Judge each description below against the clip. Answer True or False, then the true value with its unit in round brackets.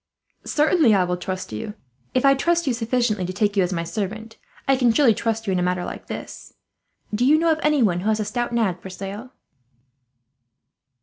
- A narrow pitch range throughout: False (5.3 semitones)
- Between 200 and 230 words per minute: True (205 wpm)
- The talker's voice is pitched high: True (220 Hz)